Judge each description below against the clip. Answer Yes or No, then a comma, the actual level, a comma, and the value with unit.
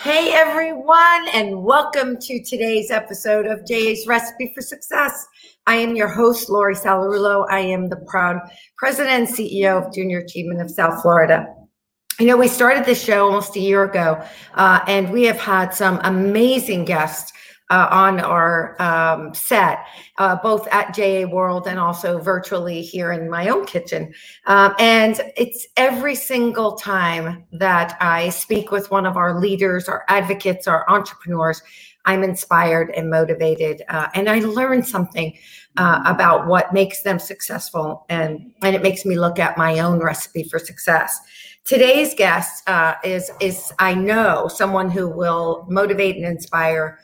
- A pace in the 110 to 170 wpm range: Yes, average, 160 wpm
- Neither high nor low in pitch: No, high, 195 Hz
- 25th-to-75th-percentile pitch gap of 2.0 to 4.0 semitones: No, average, 4.4 semitones